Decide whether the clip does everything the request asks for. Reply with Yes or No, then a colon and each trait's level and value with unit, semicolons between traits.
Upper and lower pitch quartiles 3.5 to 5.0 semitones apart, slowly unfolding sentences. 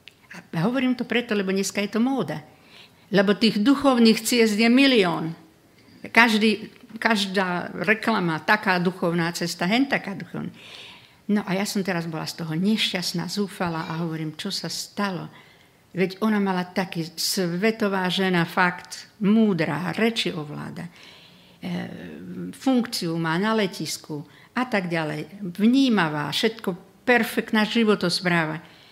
No: average, 4.6 semitones; average, 125 wpm